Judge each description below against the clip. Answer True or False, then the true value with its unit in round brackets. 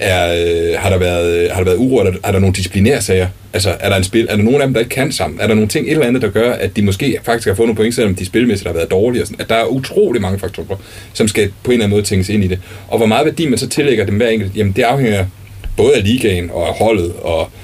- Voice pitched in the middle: False (100 Hz)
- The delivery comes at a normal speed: False (310 wpm)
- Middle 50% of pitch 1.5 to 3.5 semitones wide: True (3.2 semitones)